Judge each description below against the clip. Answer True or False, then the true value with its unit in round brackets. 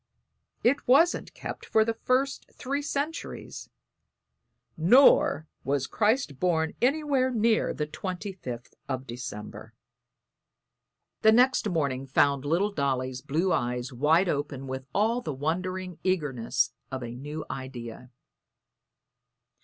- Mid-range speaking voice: True (160 Hz)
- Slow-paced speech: True (115 wpm)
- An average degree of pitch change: False (8.9 semitones)